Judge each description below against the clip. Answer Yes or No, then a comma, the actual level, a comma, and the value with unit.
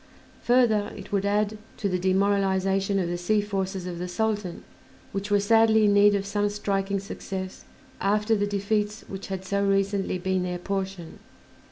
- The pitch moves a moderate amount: No, narrow, 1.5 semitones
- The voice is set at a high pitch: Yes, high, 200 Hz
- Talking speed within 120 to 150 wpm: No, average, 170 wpm